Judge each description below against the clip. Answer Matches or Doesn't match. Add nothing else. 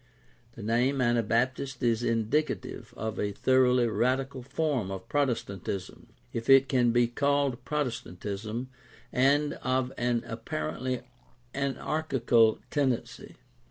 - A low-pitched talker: Matches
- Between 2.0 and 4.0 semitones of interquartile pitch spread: Matches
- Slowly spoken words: Matches